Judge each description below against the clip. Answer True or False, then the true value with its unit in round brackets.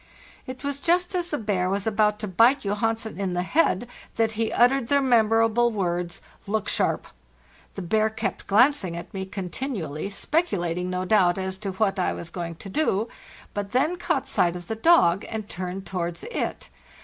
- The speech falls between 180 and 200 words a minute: True (185 wpm)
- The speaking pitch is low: False (210 Hz)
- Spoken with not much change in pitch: False (4.6 semitones)